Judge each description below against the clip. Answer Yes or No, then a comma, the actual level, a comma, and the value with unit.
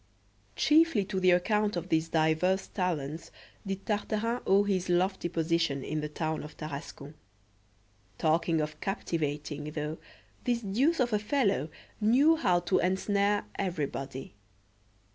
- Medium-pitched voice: Yes, medium, 180 Hz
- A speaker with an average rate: No, slow, 130 wpm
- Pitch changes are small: No, average, 4.8 semitones